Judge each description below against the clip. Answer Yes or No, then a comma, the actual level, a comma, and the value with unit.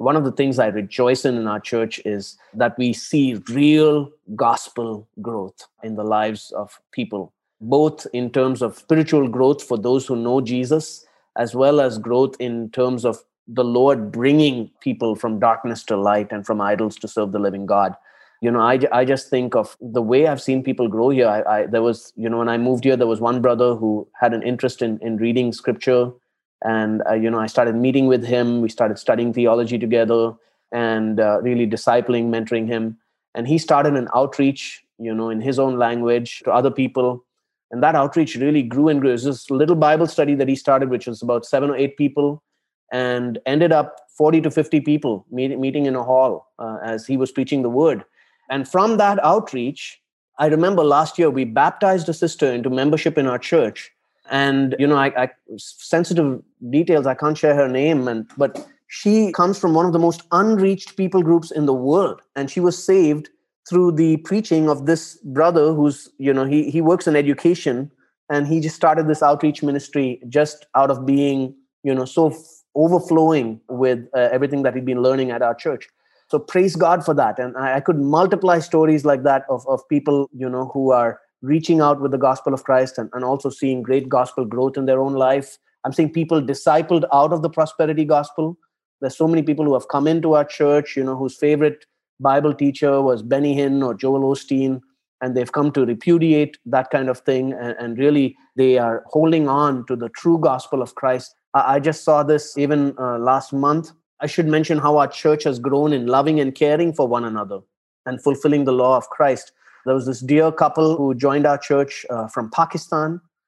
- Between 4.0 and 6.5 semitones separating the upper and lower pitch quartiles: No, average, 3.6 semitones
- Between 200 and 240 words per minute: Yes, fast, 205 wpm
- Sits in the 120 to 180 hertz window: Yes, low, 135 Hz